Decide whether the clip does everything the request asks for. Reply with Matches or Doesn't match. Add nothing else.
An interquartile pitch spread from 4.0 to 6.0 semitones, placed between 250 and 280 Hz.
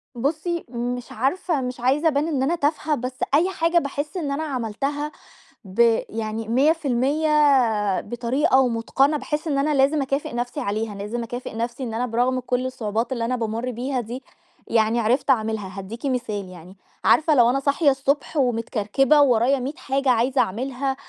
Doesn't match